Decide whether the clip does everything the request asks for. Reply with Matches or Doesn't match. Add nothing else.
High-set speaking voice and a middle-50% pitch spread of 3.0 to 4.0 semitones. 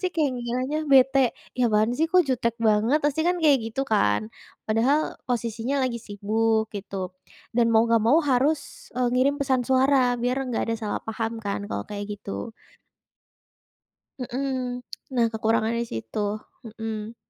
Matches